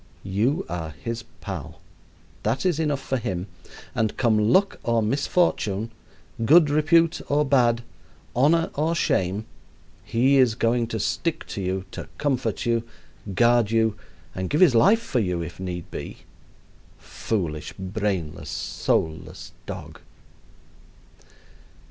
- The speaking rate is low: Yes, slow, 125 wpm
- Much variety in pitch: Yes, wide, 6.7 semitones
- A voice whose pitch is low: Yes, low, 115 Hz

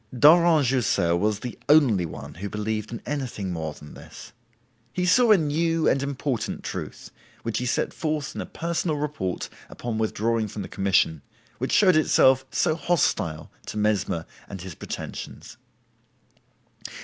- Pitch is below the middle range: Yes, low, 120 Hz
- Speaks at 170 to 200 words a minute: No, average, 150 wpm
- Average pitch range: No, wide, 7.5 semitones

